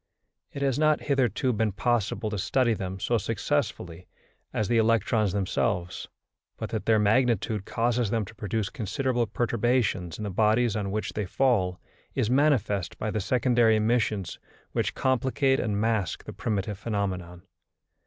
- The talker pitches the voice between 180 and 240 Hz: No, low, 110 Hz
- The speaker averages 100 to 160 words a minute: Yes, average, 150 wpm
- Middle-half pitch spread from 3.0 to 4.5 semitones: Yes, average, 3.4 semitones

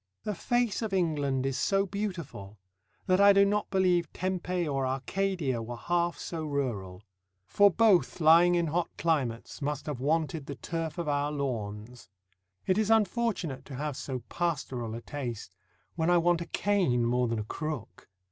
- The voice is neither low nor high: Yes, medium, 155 Hz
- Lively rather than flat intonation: Yes, wide, 5.9 semitones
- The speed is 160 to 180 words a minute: Yes, average, 165 wpm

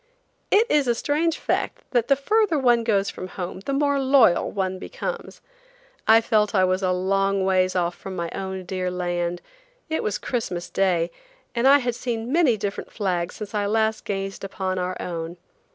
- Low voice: No, high, 200 Hz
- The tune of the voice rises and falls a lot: No, average, 4.9 semitones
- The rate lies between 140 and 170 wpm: No, average, 185 wpm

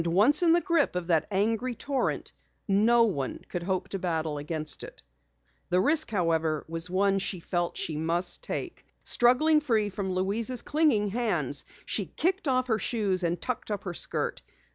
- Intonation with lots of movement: Yes, wide, 6.0 semitones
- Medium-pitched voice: No, high, 200 Hz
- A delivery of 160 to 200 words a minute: Yes, average, 170 wpm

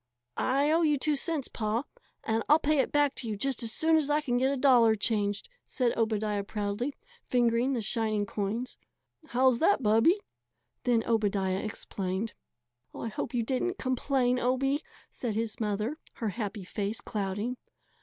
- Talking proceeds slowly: No, average, 165 wpm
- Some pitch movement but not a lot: Yes, average, 4.2 semitones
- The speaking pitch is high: Yes, high, 235 Hz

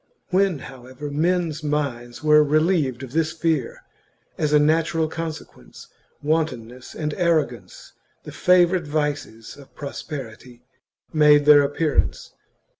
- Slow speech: Yes, slow, 115 wpm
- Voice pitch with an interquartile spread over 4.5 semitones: No, average, 3.2 semitones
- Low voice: No, medium, 150 Hz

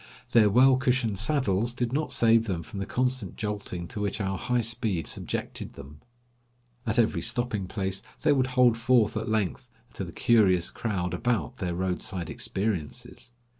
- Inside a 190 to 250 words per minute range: No, average, 165 wpm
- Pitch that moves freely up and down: No, average, 4.3 semitones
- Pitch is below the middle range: Yes, low, 110 Hz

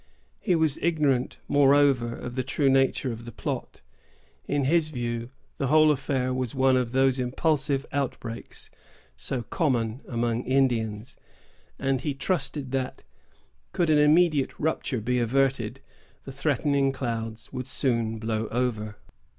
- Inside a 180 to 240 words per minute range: No, slow, 135 wpm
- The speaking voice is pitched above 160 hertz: No, low, 130 Hz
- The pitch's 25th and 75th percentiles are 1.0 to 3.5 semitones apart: Yes, average, 3.1 semitones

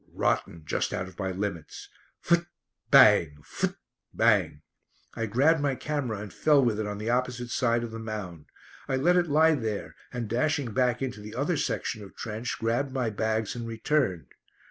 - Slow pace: No, average, 180 wpm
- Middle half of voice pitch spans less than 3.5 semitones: No, average, 4.3 semitones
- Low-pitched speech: Yes, low, 115 Hz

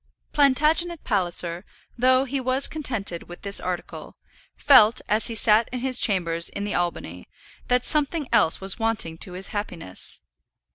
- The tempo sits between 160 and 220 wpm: No, average, 150 wpm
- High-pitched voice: Yes, high, 215 Hz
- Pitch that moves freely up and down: Yes, wide, 6.4 semitones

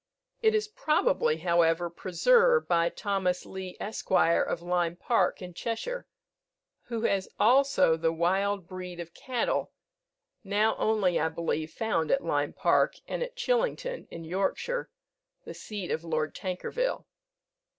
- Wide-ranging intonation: Yes, wide, 8.4 semitones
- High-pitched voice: Yes, high, 195 Hz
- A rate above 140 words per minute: No, slow, 135 wpm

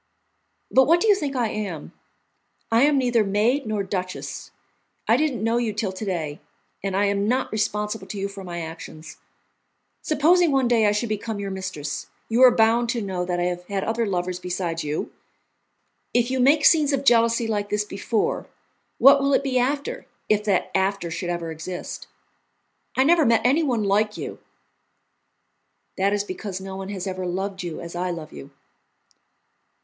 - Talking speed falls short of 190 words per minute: Yes, average, 180 wpm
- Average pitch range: Yes, average, 4.7 semitones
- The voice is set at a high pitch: Yes, high, 210 Hz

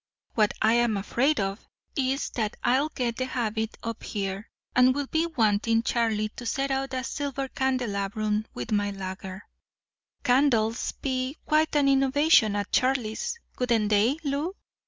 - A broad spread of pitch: No, average, 4.1 semitones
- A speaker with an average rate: Yes, average, 145 wpm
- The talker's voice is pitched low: No, high, 240 Hz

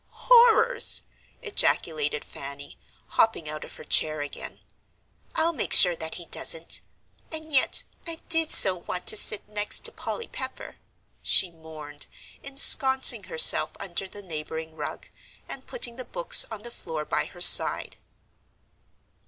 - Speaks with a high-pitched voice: Yes, high, 205 Hz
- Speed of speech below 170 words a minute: Yes, average, 140 wpm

